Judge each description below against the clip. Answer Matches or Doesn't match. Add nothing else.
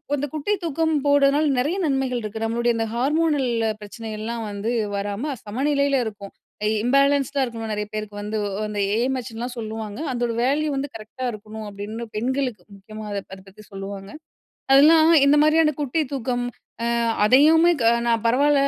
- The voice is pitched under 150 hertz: Doesn't match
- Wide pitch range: Doesn't match